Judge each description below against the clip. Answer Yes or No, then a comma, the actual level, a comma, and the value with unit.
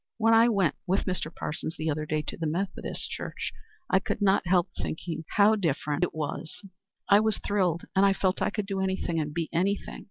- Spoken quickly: Yes, fast, 210 wpm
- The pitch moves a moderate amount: Yes, average, 3.8 semitones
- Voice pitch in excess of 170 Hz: Yes, medium, 185 Hz